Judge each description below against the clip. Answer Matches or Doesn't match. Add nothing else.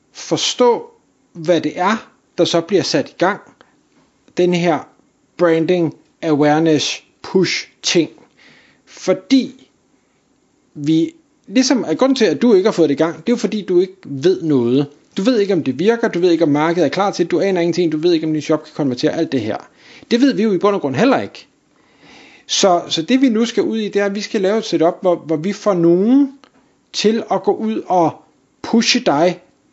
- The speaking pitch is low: Doesn't match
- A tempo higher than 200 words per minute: Matches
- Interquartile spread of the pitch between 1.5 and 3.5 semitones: Doesn't match